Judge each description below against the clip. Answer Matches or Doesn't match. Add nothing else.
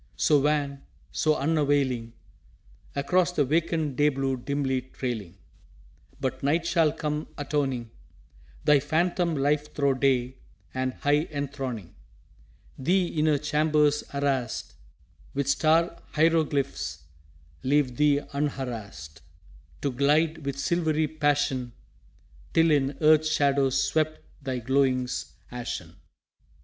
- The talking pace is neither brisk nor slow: Doesn't match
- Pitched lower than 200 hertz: Matches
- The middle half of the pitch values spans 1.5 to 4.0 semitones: Matches